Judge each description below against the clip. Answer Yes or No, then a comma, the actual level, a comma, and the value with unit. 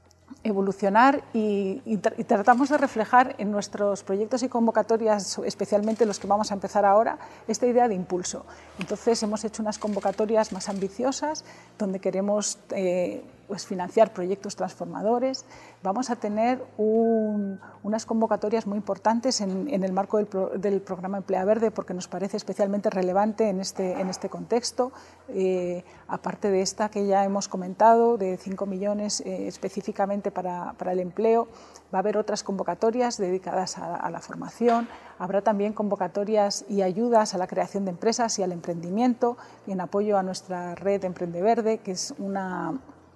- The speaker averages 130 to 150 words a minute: No, average, 165 wpm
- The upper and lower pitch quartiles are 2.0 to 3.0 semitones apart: Yes, average, 2.7 semitones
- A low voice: No, high, 205 Hz